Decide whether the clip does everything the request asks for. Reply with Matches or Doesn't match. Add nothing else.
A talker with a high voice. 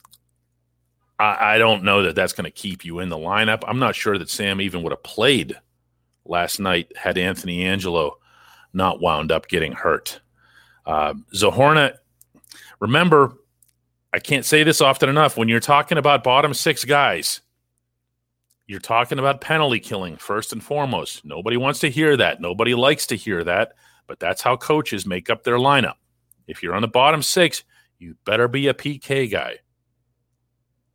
Doesn't match